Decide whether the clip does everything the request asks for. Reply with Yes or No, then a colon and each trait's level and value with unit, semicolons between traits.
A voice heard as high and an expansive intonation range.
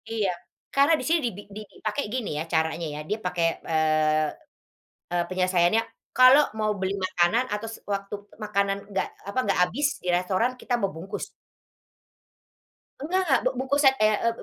Yes: high, 200 Hz; wide, 5.9 semitones